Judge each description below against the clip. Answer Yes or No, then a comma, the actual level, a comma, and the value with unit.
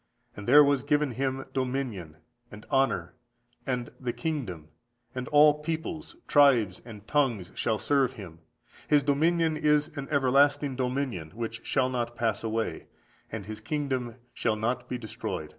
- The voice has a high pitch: No, low, 130 Hz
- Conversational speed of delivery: Yes, average, 145 wpm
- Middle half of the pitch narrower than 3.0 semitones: No, average, 4.4 semitones